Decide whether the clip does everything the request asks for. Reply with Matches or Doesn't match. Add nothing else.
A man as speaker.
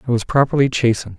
Matches